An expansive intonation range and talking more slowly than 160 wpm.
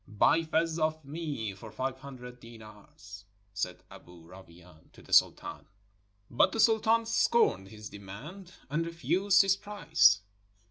Yes: wide, 8.7 semitones; slow, 135 wpm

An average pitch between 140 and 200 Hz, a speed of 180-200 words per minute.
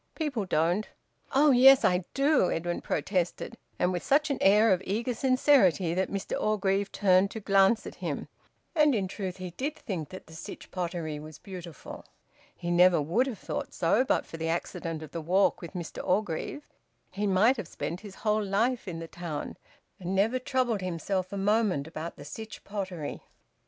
Yes: high, 190 Hz; average, 185 wpm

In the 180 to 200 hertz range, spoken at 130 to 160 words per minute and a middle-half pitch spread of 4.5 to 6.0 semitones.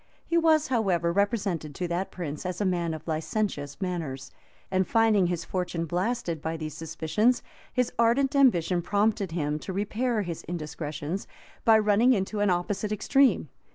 Yes: medium, 185 Hz; average, 155 wpm; average, 4.9 semitones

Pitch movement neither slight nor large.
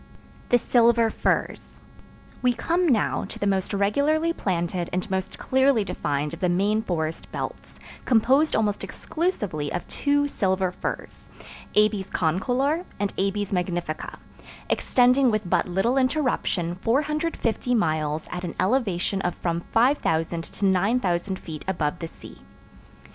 No: wide, 6.0 semitones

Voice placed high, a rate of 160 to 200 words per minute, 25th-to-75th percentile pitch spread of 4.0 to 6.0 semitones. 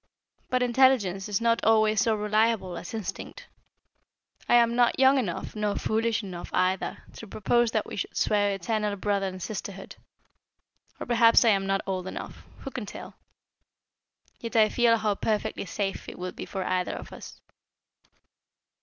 No: high, 215 Hz; average, 165 wpm; average, 3.0 semitones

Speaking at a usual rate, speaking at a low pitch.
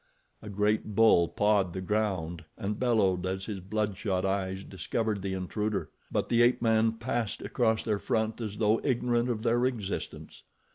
Yes: average, 160 wpm; low, 105 Hz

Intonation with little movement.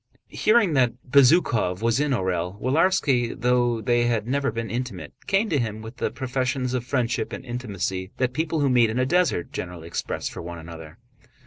No: average, 3.8 semitones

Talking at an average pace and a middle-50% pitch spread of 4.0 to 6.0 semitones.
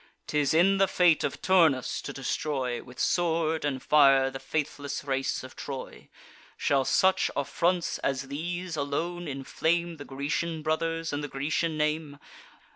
No: average, 145 wpm; average, 3.3 semitones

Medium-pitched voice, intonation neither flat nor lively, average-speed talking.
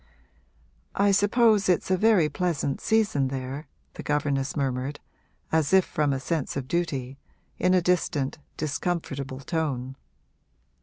No: medium, 150 Hz; average, 5.0 semitones; slow, 130 wpm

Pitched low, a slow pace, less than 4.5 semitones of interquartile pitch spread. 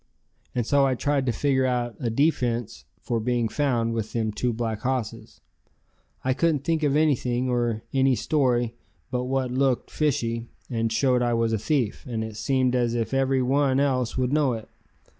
No: low, 125 Hz; average, 180 wpm; narrow, 2.6 semitones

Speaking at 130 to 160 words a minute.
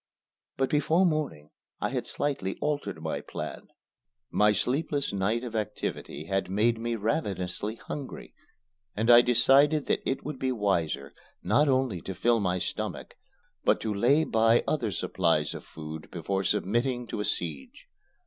Yes: average, 150 wpm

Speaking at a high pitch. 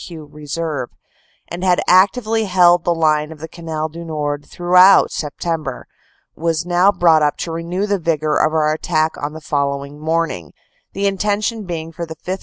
No: medium, 165 Hz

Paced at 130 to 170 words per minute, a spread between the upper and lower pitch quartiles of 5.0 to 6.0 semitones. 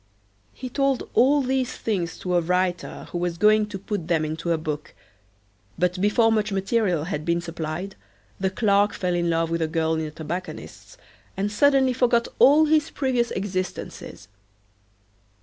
Yes: average, 165 wpm; wide, 5.5 semitones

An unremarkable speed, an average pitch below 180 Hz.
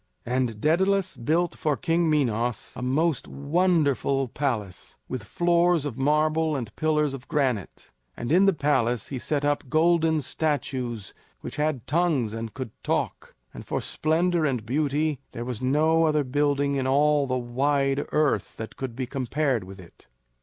Yes: average, 160 wpm; medium, 140 Hz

